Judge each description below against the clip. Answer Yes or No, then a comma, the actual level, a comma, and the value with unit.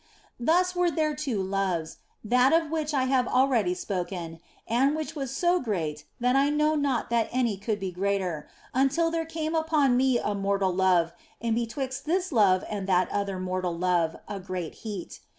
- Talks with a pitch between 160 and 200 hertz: No, high, 230 Hz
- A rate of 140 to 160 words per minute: No, average, 180 wpm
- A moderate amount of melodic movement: No, wide, 7.7 semitones